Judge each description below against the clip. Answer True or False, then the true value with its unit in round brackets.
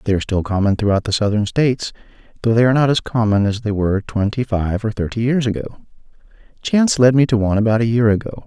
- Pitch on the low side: True (110 Hz)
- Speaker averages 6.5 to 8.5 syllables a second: True (6.9 syllables/s)